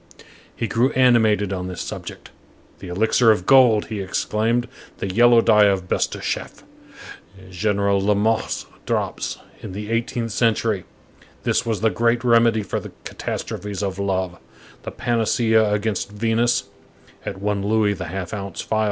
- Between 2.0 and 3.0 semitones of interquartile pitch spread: Yes, average, 2.7 semitones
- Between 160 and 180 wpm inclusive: No, average, 140 wpm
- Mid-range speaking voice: No, low, 105 Hz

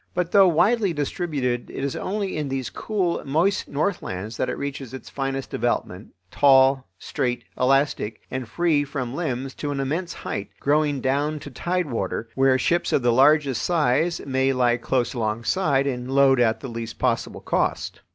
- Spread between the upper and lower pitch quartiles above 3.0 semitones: Yes, average, 3.5 semitones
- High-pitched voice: No, low, 135 Hz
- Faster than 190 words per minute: No, average, 170 wpm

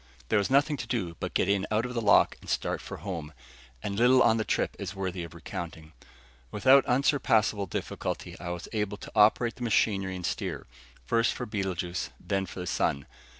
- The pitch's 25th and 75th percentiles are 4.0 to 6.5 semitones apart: Yes, average, 4.3 semitones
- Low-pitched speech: Yes, low, 100 Hz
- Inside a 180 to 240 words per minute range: Yes, average, 195 wpm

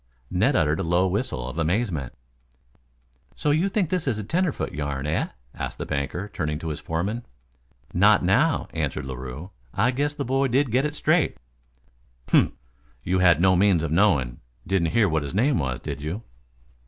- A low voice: Yes, very low, 95 Hz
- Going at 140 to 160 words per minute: No, average, 180 wpm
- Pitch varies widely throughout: Yes, wide, 8.5 semitones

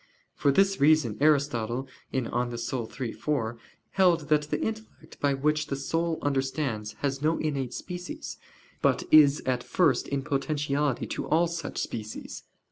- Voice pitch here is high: No, medium, 145 Hz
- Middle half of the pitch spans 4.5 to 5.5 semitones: No, average, 2.9 semitones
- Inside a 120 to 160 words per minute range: Yes, average, 145 wpm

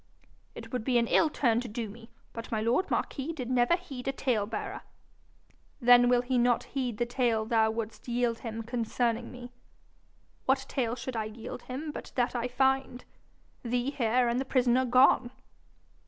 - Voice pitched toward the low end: No, high, 245 Hz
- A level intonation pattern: Yes, narrow, 1.9 semitones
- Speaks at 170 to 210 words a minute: Yes, average, 180 wpm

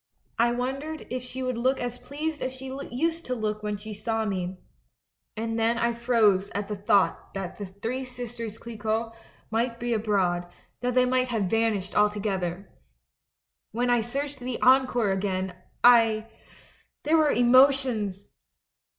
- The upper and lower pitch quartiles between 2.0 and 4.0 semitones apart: Yes, average, 3.4 semitones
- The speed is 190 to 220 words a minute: No, average, 150 wpm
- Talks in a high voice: Yes, high, 230 Hz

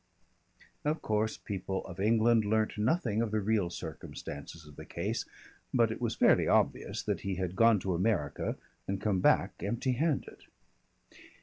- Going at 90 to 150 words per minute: No, average, 160 wpm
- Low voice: Yes, low, 105 Hz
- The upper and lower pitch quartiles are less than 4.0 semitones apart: Yes, average, 3.3 semitones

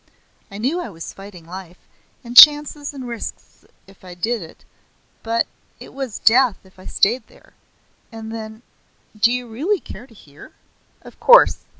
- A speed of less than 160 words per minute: No, average, 165 wpm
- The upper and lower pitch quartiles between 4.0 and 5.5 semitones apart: Yes, average, 4.9 semitones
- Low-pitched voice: No, high, 225 Hz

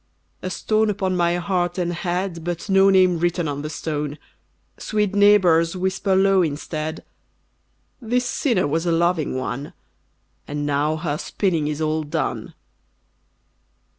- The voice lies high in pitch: No, medium, 175 Hz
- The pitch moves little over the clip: No, average, 3.6 semitones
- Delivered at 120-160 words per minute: Yes, slow, 135 wpm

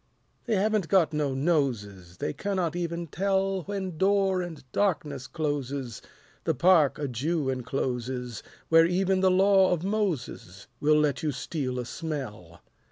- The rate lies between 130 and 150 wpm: Yes, average, 145 wpm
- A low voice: No, medium, 155 Hz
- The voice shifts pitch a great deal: Yes, wide, 6.1 semitones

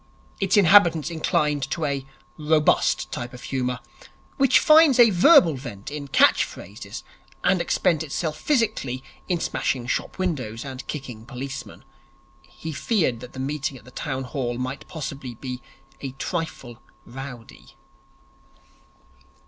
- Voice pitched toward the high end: No, medium, 140 Hz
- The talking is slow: Yes, slow, 130 wpm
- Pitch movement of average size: Yes, average, 4.6 semitones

